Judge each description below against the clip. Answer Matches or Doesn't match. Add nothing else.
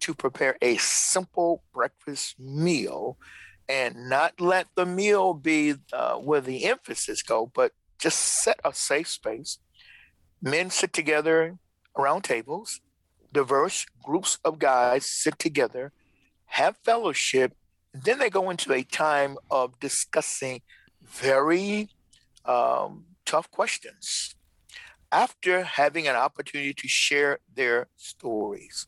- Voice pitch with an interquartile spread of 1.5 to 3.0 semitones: Doesn't match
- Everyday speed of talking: Doesn't match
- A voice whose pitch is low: Doesn't match